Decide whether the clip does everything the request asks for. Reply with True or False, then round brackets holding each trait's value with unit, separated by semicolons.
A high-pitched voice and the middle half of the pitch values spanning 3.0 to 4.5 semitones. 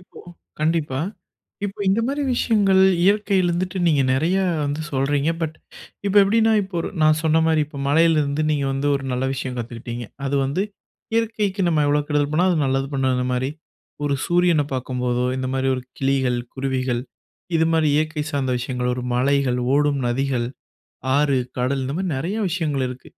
False (145 Hz; 4.2 semitones)